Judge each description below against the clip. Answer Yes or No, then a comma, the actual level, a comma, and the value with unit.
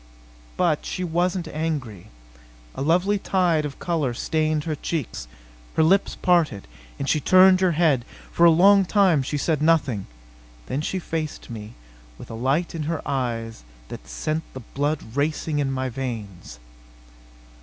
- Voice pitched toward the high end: No, medium, 155 Hz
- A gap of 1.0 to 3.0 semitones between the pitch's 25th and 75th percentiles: No, average, 4.6 semitones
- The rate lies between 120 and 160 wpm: Yes, average, 155 wpm